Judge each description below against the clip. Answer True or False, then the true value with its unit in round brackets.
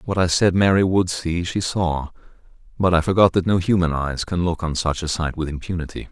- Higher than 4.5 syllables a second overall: True (5.4 syllables/s)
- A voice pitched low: True (85 Hz)